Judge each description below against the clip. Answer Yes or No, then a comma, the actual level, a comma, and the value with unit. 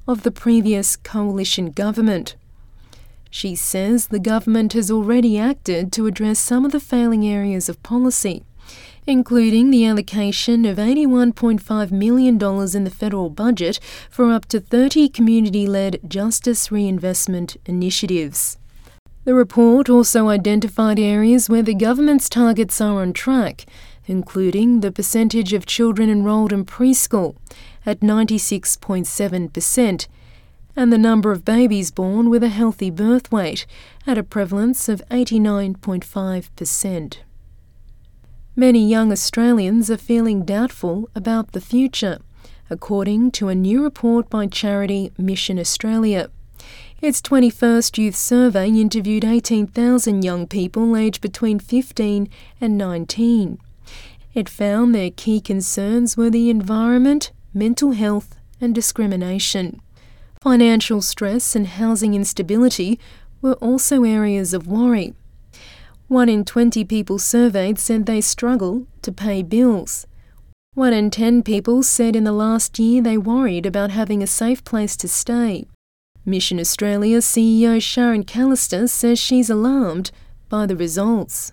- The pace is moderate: No, slow, 125 wpm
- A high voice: Yes, high, 220 Hz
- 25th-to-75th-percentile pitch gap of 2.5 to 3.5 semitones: Yes, average, 3.1 semitones